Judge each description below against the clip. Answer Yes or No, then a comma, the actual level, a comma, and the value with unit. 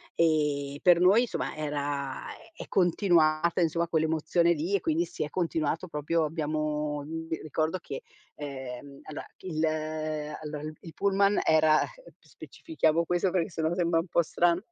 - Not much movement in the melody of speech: Yes, narrow, 2.2 semitones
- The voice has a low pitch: No, medium, 160 Hz